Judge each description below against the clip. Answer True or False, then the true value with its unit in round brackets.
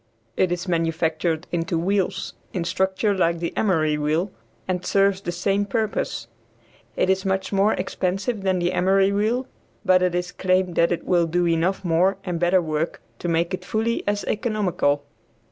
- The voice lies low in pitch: False (185 Hz)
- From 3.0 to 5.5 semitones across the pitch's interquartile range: False (2.5 semitones)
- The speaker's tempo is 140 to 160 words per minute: False (170 wpm)